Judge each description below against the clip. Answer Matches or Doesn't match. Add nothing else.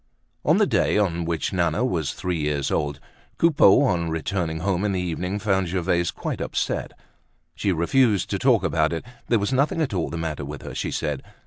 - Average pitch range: Matches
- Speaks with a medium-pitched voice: Doesn't match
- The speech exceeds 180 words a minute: Matches